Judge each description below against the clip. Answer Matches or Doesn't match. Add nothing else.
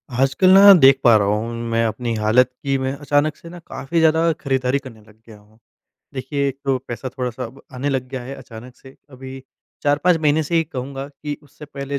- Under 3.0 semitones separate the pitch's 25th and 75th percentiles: Matches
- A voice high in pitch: Doesn't match